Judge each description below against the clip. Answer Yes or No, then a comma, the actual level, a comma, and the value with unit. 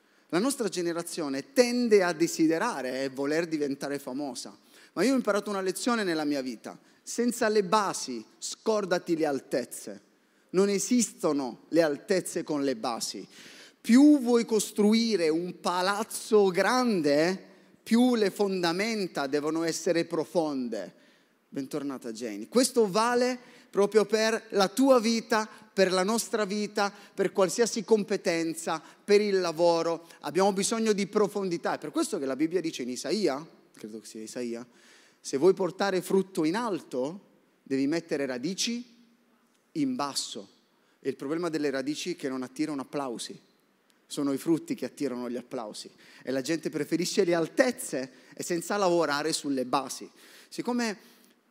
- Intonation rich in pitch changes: Yes, wide, 6.5 semitones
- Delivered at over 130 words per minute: Yes, average, 140 wpm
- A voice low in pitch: No, medium, 185 Hz